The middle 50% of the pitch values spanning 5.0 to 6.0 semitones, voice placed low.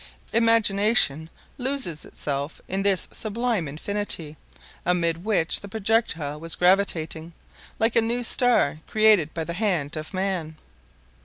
No: wide, 5.5 semitones; high, 190 Hz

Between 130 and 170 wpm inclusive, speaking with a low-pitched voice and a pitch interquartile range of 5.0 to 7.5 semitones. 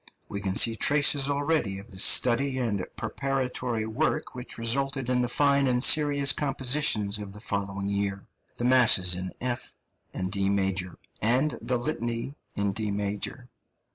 Yes: average, 155 wpm; low, 120 Hz; average, 5.3 semitones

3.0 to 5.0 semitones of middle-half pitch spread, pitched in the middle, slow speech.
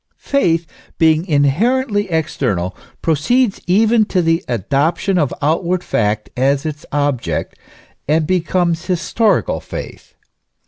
Yes: average, 4.7 semitones; medium, 165 Hz; slow, 110 wpm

